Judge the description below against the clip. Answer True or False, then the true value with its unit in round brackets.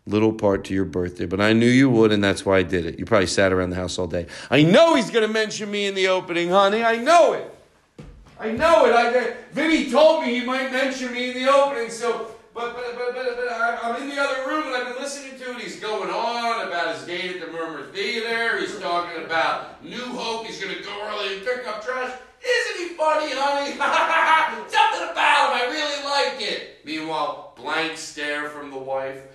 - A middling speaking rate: False (225 wpm)